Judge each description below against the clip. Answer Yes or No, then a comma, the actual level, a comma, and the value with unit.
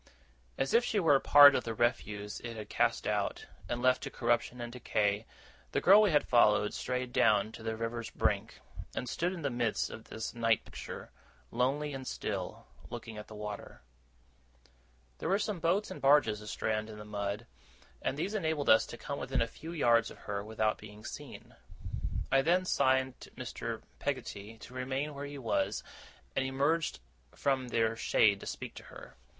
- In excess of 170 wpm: Yes, average, 185 wpm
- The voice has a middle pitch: No, low, 120 Hz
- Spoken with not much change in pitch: No, average, 4.6 semitones